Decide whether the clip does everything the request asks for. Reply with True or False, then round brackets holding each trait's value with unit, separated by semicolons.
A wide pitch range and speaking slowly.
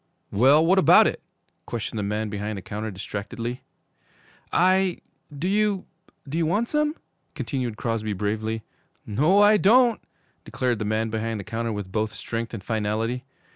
False (8.1 semitones; 155 wpm)